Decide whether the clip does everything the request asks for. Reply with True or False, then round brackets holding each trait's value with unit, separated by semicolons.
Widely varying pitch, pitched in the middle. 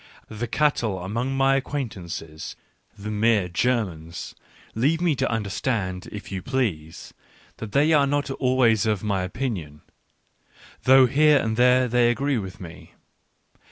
False (5.7 semitones; 115 Hz)